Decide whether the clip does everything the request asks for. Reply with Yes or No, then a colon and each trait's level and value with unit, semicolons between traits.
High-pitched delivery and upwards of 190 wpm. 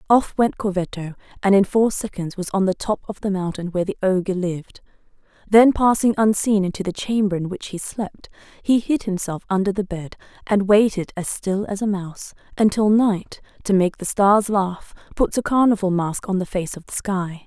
Yes: high, 195 Hz; average, 200 wpm